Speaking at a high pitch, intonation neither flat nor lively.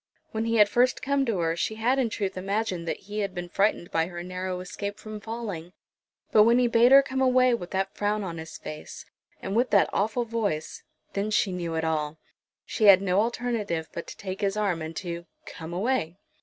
Yes: high, 200 Hz; average, 4.6 semitones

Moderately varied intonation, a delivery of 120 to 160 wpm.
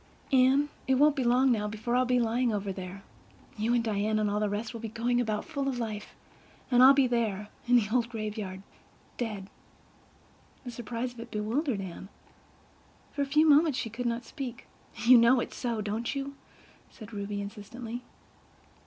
No: average, 3.2 semitones; average, 175 wpm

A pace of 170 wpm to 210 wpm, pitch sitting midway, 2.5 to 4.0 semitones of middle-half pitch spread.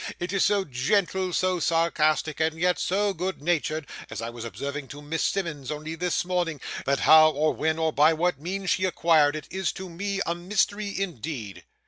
Yes: average, 190 wpm; medium, 165 Hz; average, 3.5 semitones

